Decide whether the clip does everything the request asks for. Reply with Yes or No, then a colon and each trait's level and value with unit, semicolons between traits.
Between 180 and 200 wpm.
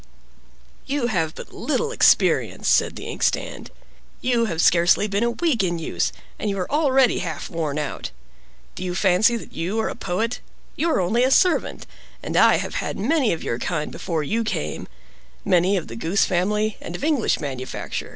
Yes: average, 185 wpm